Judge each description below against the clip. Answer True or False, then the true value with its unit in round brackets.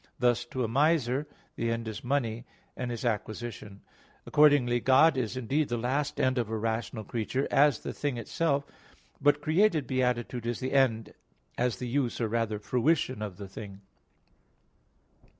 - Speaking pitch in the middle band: False (125 Hz)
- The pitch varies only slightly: False (3.4 semitones)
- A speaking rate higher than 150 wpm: True (160 wpm)